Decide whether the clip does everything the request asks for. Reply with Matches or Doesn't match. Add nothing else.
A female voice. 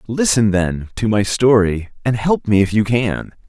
Doesn't match